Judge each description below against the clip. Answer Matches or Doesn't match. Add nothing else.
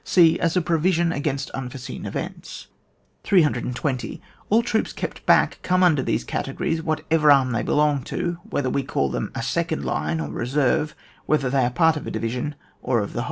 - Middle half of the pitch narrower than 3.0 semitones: Doesn't match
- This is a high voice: Doesn't match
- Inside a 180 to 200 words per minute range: Matches